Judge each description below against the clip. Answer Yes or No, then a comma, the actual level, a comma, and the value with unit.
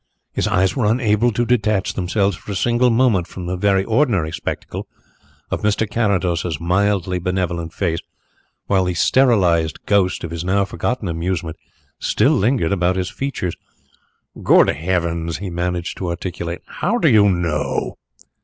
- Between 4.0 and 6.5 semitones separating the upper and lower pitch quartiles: No, average, 3.6 semitones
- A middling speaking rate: Yes, average, 150 wpm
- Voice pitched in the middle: No, very low, 95 Hz